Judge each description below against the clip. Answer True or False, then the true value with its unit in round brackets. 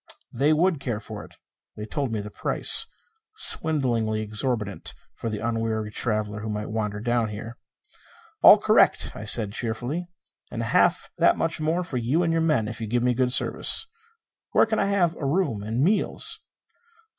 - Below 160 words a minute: False (175 wpm)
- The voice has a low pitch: True (120 Hz)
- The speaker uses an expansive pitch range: True (6.3 semitones)